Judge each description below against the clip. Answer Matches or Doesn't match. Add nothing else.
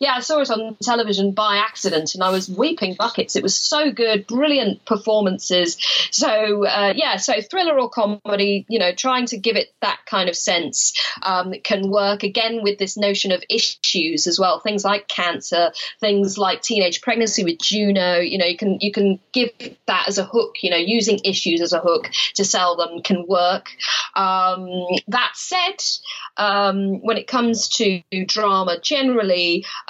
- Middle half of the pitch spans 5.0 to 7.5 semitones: Doesn't match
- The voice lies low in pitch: Doesn't match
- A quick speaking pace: Doesn't match